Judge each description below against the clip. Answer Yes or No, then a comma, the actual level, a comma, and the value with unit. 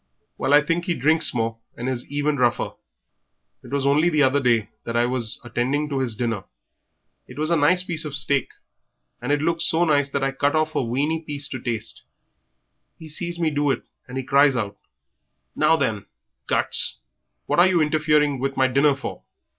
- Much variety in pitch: No, average, 3.4 semitones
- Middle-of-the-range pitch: Yes, medium, 145 Hz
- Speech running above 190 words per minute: Yes, average, 200 wpm